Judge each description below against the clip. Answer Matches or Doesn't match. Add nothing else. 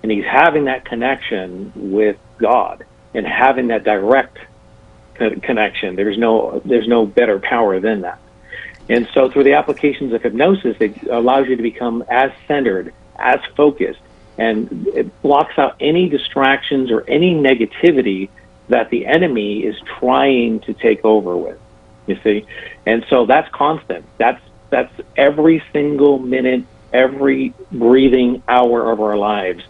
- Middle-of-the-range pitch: Doesn't match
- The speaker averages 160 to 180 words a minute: Doesn't match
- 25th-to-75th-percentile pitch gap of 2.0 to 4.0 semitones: Matches